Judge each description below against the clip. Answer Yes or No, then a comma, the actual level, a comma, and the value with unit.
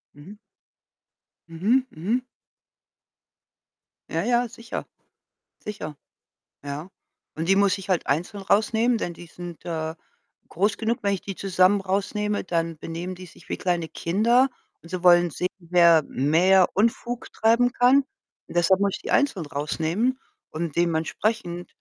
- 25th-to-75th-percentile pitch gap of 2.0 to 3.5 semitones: No, average, 4.3 semitones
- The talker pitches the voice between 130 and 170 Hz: No, medium, 185 Hz